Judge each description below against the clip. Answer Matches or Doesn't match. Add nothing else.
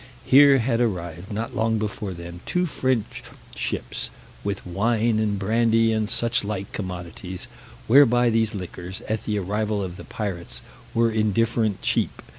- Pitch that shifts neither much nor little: Matches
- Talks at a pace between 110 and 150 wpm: Matches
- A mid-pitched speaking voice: Doesn't match